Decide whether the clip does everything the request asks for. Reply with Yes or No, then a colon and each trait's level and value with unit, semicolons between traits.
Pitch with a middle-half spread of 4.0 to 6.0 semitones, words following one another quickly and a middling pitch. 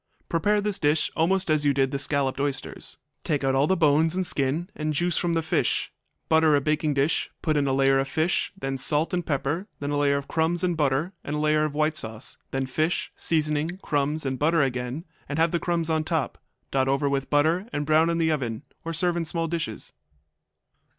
No: average, 2.9 semitones; fast, 215 wpm; medium, 155 Hz